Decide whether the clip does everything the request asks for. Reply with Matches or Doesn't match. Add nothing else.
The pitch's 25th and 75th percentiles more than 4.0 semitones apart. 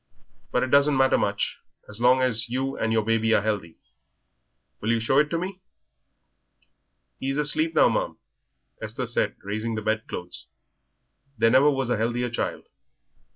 Doesn't match